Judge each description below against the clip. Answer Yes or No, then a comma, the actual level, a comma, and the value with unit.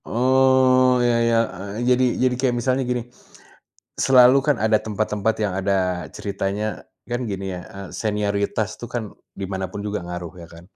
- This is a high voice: No, low, 110 Hz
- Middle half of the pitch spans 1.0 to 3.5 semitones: No, average, 4.3 semitones